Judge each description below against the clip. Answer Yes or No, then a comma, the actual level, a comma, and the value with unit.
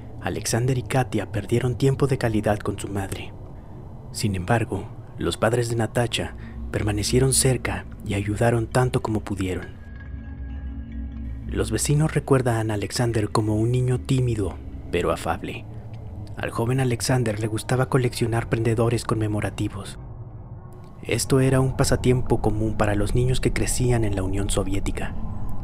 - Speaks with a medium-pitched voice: No, low, 110 Hz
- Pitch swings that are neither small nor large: Yes, average, 3.3 semitones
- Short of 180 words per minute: Yes, average, 130 wpm